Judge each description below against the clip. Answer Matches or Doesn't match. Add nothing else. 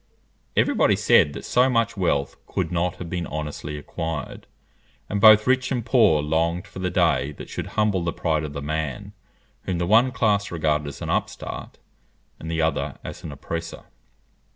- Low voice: Matches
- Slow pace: Doesn't match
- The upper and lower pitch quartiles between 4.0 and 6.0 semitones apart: Matches